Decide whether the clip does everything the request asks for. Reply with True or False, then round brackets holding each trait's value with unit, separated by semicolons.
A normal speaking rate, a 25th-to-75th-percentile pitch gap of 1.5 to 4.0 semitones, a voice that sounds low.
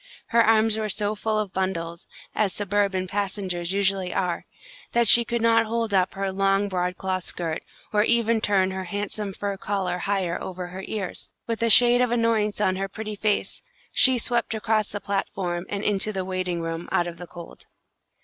False (185 wpm; 2.7 semitones; 200 Hz)